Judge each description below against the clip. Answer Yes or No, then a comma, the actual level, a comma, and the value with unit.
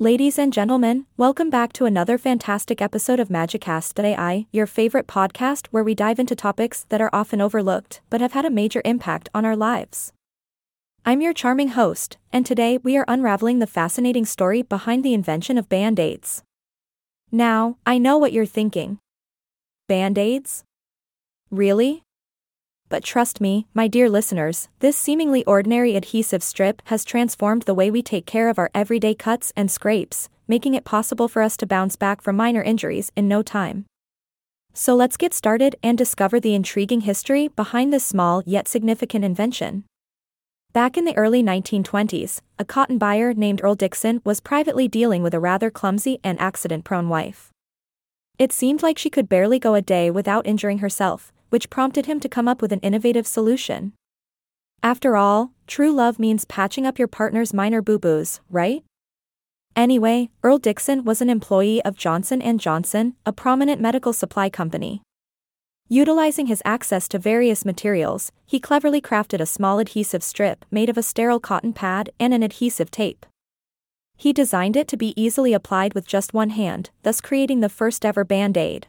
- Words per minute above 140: Yes, average, 170 wpm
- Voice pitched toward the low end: No, high, 220 Hz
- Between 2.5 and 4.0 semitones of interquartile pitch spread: Yes, average, 3.5 semitones